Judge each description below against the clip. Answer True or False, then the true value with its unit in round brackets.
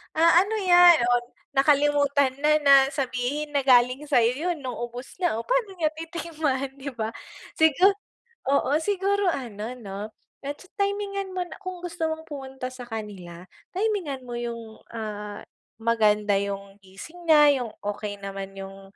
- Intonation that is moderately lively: False (6.8 semitones)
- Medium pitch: False (270 Hz)